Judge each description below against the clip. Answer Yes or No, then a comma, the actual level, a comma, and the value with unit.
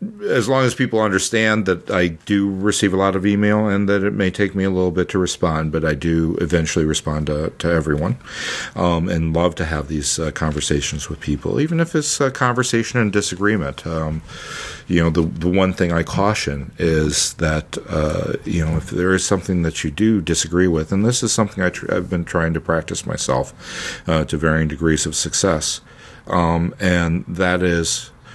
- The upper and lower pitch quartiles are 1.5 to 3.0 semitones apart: No, average, 3.9 semitones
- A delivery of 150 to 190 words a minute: No, average, 200 wpm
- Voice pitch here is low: Yes, very low, 85 Hz